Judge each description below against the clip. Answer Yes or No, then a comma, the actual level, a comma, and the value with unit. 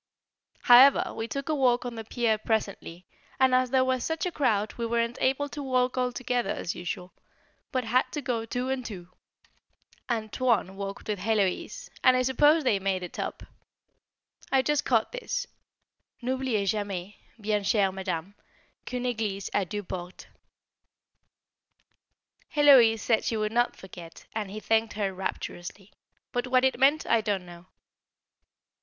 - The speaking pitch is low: No, high, 225 Hz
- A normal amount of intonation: Yes, average, 4.3 semitones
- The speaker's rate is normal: Yes, average, 155 wpm